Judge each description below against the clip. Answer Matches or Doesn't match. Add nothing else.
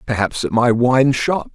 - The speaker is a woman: Doesn't match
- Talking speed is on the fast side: Doesn't match